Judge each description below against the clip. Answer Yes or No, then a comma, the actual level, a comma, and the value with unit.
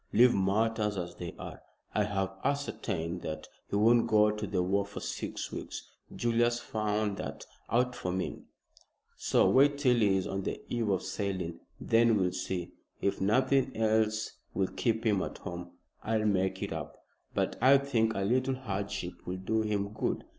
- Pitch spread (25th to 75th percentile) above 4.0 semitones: No, average, 3.4 semitones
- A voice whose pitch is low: Yes, low, 105 Hz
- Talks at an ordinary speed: Yes, average, 175 wpm